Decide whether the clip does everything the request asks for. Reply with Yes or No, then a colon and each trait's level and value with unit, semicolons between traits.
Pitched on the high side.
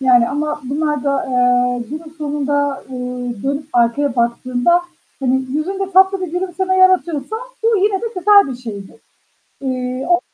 Yes: very high, 285 Hz